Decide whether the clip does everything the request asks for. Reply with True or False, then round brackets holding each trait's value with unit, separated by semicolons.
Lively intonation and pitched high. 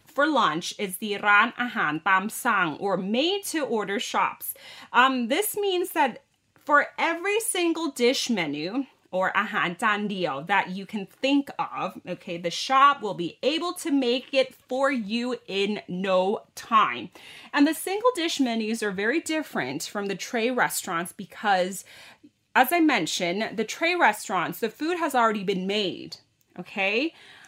True (6.8 semitones; 235 Hz)